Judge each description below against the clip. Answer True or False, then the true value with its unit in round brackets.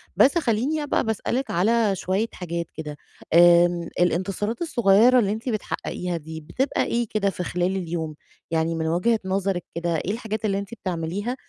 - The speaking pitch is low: False (195 Hz)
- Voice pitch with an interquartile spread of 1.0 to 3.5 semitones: False (4.7 semitones)